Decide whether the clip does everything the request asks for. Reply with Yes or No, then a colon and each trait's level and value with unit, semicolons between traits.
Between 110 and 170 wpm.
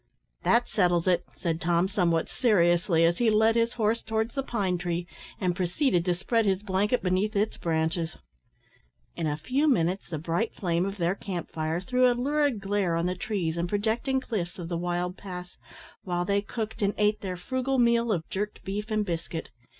No: average, 190 wpm